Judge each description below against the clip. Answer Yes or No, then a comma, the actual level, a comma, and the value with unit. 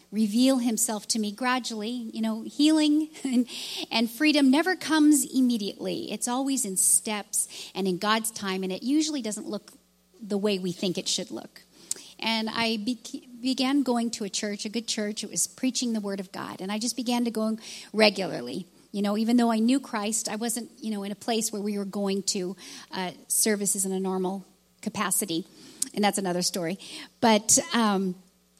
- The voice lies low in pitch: No, high, 215 Hz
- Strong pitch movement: No, average, 3.8 semitones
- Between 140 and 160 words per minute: No, average, 190 wpm